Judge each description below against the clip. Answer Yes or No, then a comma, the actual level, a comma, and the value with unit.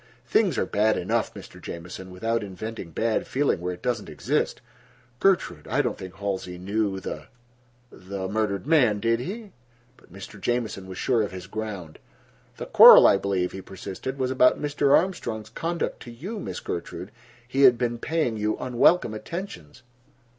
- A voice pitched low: Yes, low, 110 Hz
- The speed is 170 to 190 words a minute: No, average, 160 wpm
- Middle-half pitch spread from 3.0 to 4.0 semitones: No, average, 4.9 semitones